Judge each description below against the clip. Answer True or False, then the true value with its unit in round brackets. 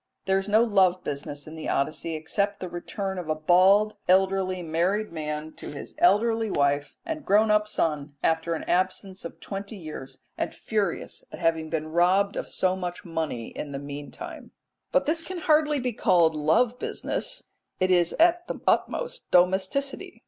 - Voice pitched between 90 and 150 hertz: False (185 Hz)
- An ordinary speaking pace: True (170 wpm)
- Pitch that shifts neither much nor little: True (4.9 semitones)